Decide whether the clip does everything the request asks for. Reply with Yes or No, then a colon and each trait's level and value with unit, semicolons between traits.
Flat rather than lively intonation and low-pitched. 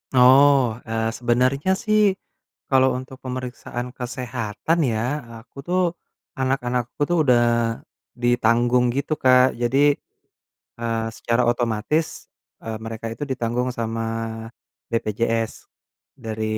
Yes: narrow, 2.2 semitones; low, 120 Hz